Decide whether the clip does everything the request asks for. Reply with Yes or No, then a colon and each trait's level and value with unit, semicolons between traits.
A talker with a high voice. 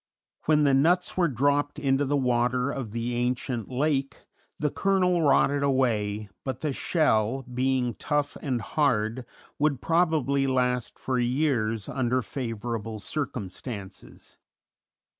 No: low, 130 Hz